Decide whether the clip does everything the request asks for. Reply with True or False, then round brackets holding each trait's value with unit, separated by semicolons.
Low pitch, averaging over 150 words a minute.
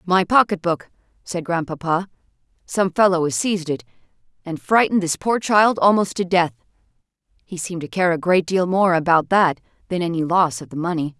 False (175 Hz; 180 wpm)